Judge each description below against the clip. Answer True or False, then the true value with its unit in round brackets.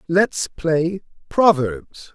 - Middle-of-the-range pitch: True (165 Hz)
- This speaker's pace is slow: True (85 wpm)